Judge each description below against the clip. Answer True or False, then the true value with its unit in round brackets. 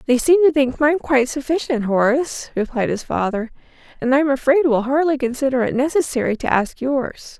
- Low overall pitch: False (270 Hz)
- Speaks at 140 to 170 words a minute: False (180 wpm)